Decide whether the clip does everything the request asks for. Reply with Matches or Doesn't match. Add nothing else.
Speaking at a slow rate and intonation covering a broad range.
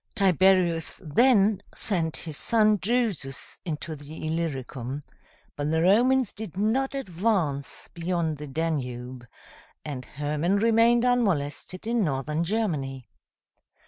Matches